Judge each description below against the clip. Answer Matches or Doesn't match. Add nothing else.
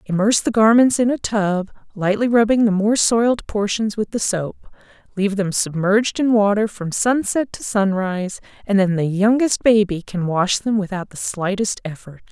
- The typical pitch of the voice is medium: Doesn't match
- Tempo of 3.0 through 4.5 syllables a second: Doesn't match